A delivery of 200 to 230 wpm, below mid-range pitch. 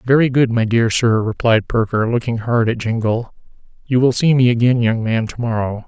Yes: fast, 205 wpm; low, 115 Hz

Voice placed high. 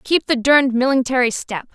Yes: very high, 255 Hz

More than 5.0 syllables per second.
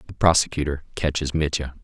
Yes: 6.0 syllables/s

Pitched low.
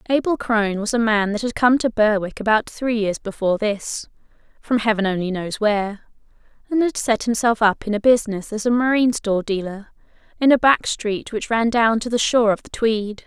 No: high, 220 Hz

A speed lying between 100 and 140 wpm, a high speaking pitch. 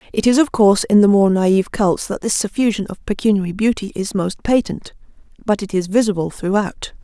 No: average, 195 wpm; high, 205 Hz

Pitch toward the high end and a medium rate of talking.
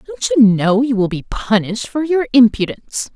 Yes: high, 235 Hz; average, 190 wpm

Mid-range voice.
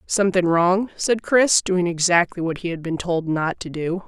Yes: medium, 175 Hz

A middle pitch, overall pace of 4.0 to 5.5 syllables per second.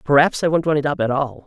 No: medium, 145 Hz; 6.0 syllables/s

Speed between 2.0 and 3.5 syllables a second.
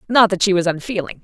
No: 6.7 syllables/s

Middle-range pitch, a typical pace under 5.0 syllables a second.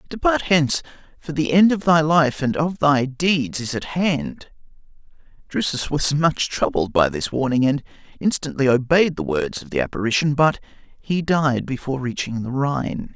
Yes: medium, 150 Hz; 4.8 syllables/s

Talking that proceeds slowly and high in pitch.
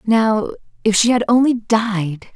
Yes: slow, 125 wpm; high, 220 Hz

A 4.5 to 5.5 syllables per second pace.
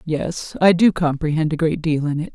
Yes: 5.1 syllables/s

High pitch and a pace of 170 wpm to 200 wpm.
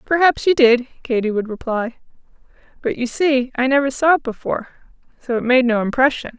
Yes: very high, 255 Hz; average, 180 wpm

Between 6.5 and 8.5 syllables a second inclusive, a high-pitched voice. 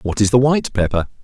No: 6.9 syllables/s; low, 115 Hz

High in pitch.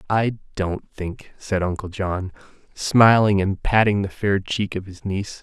No: low, 100 Hz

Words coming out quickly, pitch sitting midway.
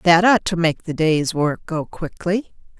No: average, 195 wpm; medium, 170 Hz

